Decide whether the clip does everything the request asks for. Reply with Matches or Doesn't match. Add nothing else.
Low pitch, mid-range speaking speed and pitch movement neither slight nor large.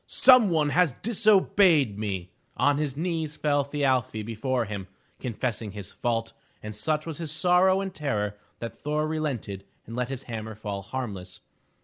Doesn't match